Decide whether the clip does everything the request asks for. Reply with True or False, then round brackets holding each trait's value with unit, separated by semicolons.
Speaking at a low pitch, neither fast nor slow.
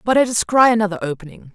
False (205 Hz; 195 wpm)